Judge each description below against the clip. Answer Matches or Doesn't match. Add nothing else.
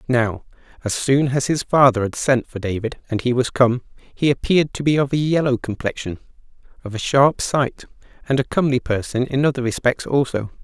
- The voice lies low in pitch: Matches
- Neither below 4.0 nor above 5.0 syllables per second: Doesn't match